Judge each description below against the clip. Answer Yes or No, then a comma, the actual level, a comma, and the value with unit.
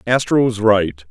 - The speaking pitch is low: Yes, low, 110 Hz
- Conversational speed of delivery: Yes, average, 160 wpm